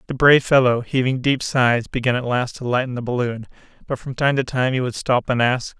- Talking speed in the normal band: No, fast, 240 wpm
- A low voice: Yes, low, 125 Hz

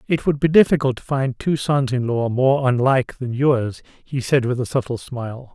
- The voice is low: Yes, low, 130 Hz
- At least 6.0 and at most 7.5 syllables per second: No, 4.9 syllables/s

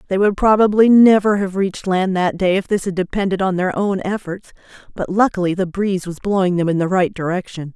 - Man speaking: No, female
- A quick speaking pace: Yes, fast, 215 wpm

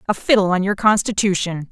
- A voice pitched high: Yes, high, 195 Hz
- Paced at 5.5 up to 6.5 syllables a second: Yes, 5.9 syllables/s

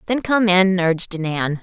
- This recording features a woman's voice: Yes, female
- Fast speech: No, average, 185 wpm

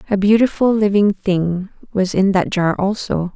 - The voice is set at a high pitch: Yes, high, 200 Hz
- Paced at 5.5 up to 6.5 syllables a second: No, 4.5 syllables/s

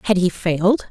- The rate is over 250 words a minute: No, average, 200 wpm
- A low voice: No, high, 190 Hz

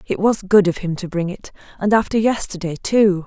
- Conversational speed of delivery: No, fast, 220 wpm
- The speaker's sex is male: No, female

